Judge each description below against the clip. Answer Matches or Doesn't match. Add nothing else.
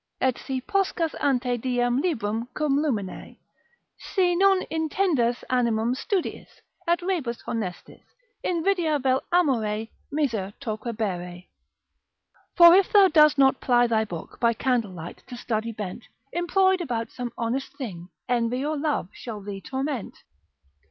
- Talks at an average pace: Doesn't match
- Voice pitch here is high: Matches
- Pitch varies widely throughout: Matches